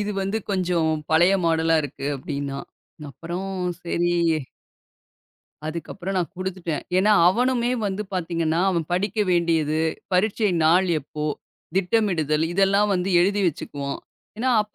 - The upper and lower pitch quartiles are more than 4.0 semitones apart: No, average, 3.4 semitones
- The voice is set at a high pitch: No, medium, 175 Hz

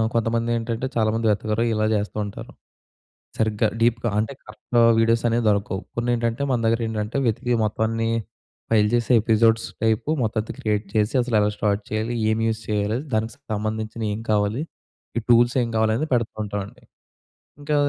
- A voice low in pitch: Yes, low, 110 Hz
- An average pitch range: No, narrow, 1.4 semitones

